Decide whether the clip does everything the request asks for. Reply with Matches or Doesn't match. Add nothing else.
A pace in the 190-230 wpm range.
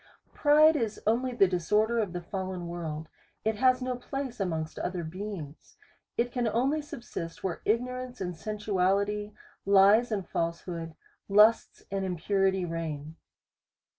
Doesn't match